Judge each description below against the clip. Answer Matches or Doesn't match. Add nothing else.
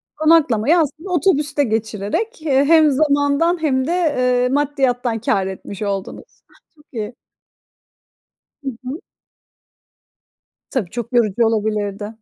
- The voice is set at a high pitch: Matches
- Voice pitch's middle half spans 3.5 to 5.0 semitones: Doesn't match